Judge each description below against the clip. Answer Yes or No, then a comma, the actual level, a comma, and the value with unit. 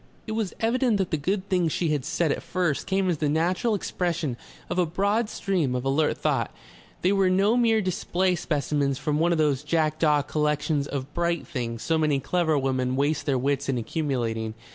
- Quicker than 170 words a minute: Yes, average, 195 wpm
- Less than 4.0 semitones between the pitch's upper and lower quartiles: No, average, 4.6 semitones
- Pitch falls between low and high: Yes, medium, 155 Hz